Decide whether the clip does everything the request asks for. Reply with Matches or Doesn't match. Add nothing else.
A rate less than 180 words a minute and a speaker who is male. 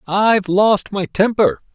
Matches